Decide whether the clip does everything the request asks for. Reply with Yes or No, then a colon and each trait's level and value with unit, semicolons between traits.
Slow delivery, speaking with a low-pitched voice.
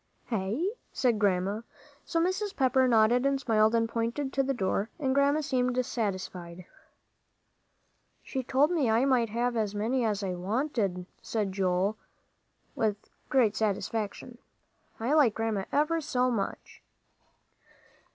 No: slow, 130 wpm; high, 230 Hz